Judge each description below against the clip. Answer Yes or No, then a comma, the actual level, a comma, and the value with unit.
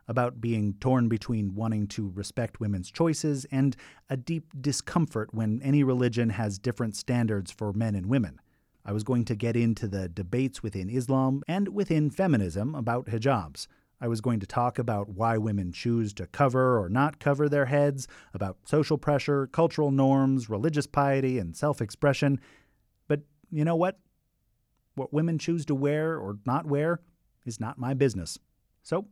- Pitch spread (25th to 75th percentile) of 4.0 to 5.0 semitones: Yes, average, 4.7 semitones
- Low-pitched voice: Yes, low, 125 Hz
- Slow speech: No, average, 165 wpm